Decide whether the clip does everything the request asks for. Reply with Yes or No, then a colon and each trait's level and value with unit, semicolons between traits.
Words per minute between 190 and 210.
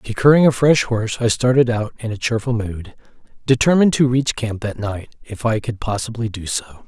Yes: average, 200 wpm